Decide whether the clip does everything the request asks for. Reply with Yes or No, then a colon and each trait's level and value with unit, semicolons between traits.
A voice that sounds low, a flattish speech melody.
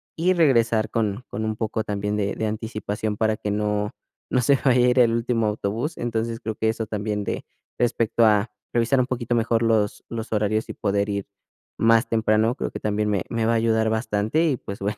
Yes: low, 110 Hz; narrow, 1.9 semitones